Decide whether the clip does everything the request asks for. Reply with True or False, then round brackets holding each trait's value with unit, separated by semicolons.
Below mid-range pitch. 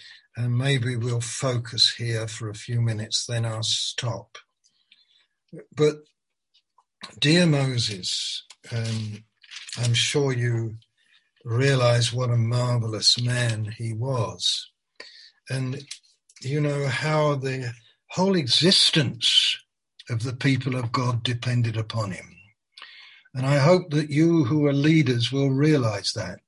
True (125 Hz)